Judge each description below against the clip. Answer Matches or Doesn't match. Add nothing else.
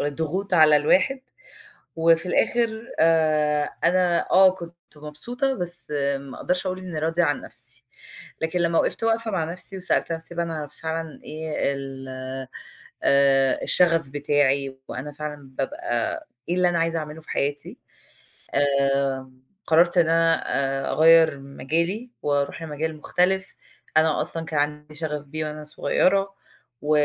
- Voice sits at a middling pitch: Matches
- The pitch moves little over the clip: Doesn't match